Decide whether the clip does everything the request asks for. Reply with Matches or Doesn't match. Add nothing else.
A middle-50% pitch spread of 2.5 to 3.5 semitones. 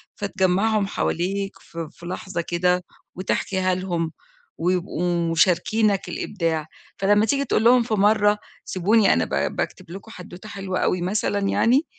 Matches